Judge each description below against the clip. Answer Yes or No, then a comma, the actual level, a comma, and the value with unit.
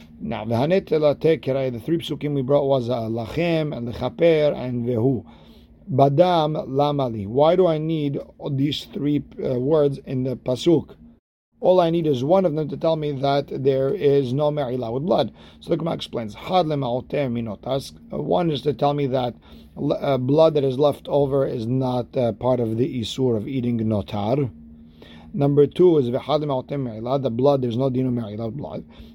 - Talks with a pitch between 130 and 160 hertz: Yes, low, 135 Hz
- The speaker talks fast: No, average, 165 wpm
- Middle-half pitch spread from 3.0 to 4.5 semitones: Yes, average, 3.6 semitones